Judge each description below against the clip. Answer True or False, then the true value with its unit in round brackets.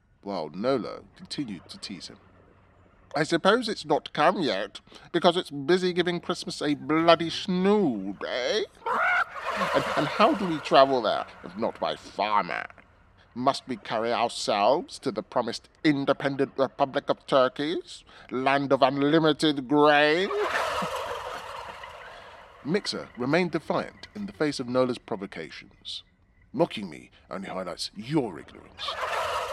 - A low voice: False (150 Hz)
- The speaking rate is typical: False (125 wpm)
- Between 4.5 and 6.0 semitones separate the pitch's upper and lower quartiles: True (5.2 semitones)